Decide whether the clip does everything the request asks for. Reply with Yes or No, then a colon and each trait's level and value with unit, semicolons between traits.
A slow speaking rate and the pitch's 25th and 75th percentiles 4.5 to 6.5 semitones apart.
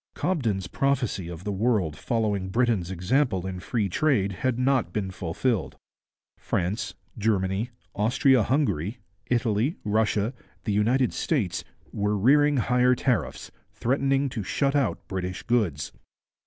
Yes: slow, 125 wpm; average, 5.1 semitones